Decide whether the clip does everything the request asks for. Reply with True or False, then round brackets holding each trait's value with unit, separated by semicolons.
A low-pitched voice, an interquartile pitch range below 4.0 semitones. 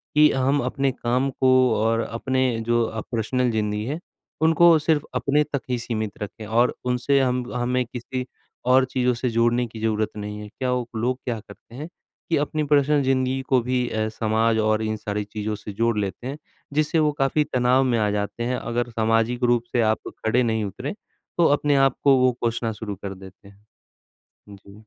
True (120 Hz; 3.1 semitones)